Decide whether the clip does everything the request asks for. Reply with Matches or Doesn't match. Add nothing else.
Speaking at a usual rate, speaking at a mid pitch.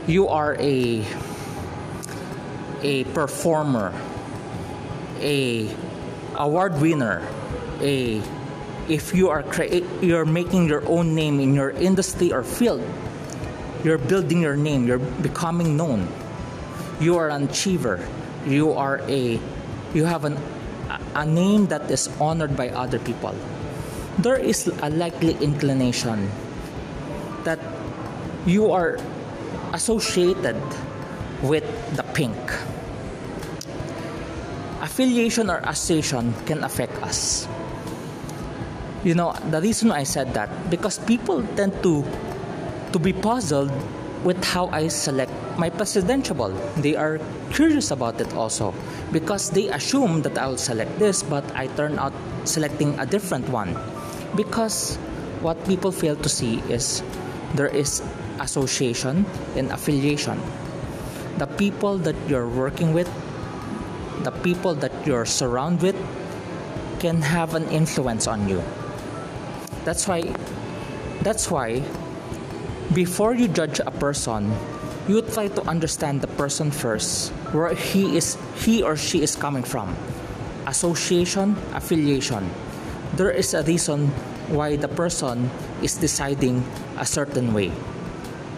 Doesn't match